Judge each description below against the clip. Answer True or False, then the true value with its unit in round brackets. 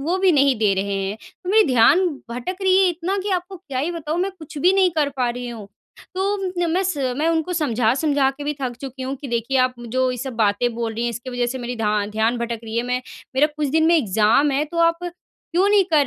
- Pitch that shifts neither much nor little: False (6.2 semitones)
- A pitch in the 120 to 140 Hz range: False (275 Hz)